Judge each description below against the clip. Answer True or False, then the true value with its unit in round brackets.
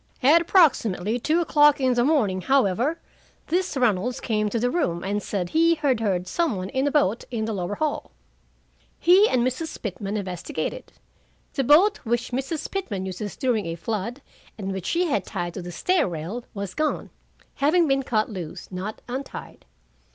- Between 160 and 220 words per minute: True (175 wpm)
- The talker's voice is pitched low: False (240 Hz)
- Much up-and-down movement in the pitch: True (7.2 semitones)